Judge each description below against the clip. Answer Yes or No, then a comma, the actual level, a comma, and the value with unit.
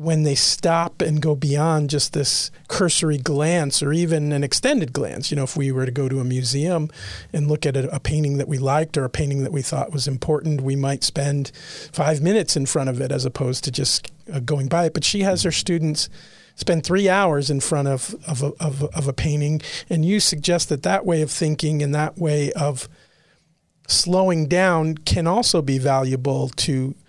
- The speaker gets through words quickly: Yes, fast, 210 wpm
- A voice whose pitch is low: No, medium, 150 Hz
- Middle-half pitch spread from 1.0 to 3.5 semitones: Yes, average, 2.8 semitones